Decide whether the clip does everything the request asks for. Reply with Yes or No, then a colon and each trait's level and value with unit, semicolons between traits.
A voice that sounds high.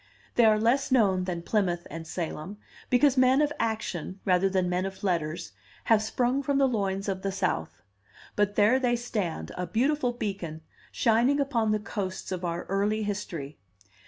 Yes: high, 205 Hz